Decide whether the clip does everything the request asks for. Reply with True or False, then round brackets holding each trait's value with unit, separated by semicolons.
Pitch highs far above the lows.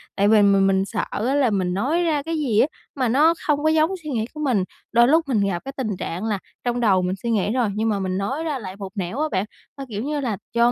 True (6.2 semitones)